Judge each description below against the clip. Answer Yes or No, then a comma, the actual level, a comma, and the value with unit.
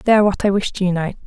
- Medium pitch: No, high, 195 Hz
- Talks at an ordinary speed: No, fast, 330 wpm